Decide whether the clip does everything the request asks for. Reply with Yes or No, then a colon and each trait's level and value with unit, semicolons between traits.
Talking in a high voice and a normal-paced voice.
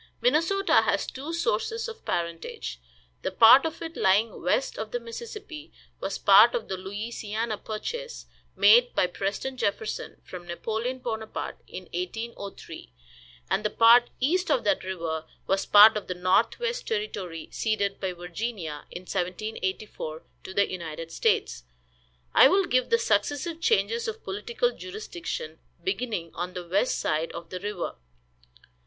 Yes: high, 220 Hz; average, 145 wpm